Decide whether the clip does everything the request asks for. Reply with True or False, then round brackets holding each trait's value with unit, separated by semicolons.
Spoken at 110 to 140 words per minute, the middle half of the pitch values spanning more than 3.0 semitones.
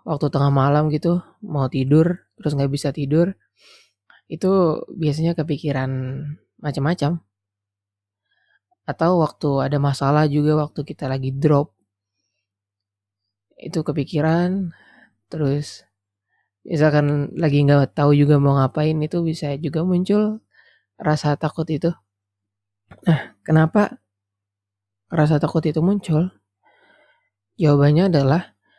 False (100 wpm; 3.5 semitones)